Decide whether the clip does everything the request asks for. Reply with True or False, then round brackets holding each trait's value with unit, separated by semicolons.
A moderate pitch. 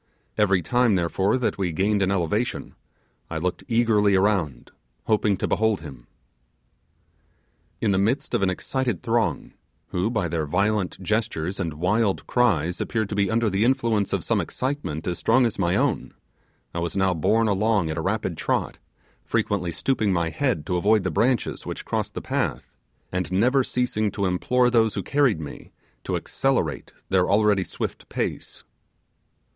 False (100 Hz)